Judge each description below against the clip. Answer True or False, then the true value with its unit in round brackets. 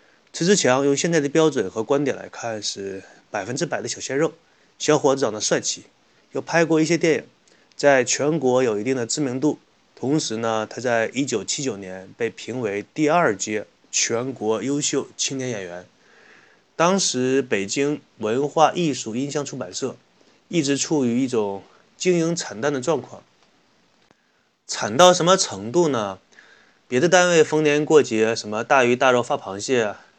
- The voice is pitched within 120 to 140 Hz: True (135 Hz)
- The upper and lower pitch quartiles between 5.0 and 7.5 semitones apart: True (5.4 semitones)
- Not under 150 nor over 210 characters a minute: False (235 characters per minute)